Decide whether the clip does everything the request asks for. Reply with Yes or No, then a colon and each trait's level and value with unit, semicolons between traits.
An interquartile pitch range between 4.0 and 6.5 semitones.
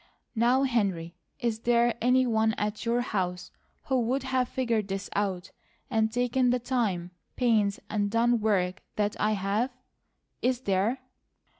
No: average, 3.5 semitones